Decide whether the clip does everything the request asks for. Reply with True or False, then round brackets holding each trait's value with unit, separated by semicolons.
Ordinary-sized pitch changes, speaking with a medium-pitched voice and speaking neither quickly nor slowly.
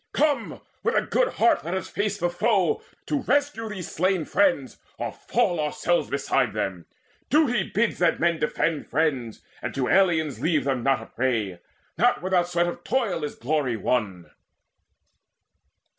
False (6.9 semitones; 175 Hz; 160 wpm)